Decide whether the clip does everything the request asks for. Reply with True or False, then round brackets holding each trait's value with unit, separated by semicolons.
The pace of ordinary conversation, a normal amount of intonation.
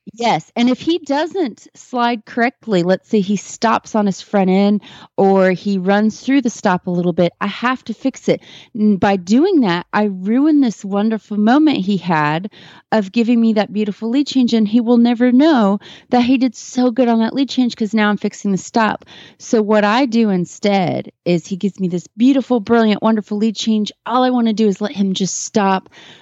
False (210 wpm; 3.5 semitones)